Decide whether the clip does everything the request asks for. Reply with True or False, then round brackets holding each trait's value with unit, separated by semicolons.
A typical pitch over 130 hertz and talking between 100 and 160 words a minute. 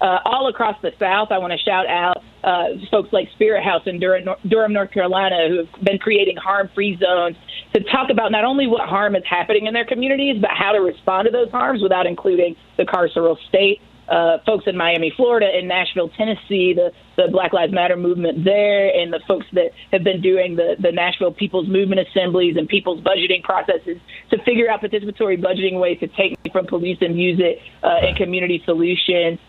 False (190 Hz; 200 wpm)